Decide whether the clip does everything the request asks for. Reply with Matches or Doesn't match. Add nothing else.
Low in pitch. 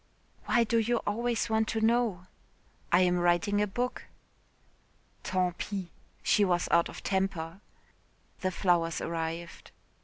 Doesn't match